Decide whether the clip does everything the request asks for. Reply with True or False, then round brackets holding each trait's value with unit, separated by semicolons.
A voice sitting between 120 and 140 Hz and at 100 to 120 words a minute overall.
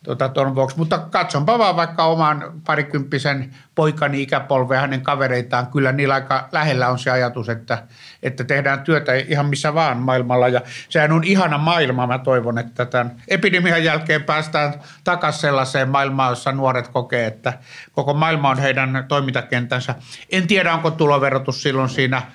False (135 Hz; 155 wpm)